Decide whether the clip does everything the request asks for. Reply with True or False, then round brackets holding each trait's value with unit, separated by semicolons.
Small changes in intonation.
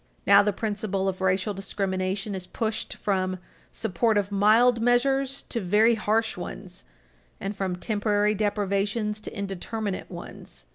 True (2.3 semitones)